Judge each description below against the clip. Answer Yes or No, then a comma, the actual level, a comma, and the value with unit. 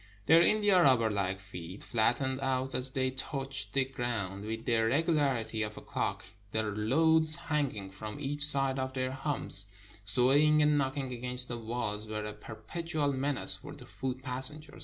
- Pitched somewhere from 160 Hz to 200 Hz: No, low, 130 Hz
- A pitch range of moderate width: Yes, average, 4.7 semitones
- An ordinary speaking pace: Yes, average, 165 wpm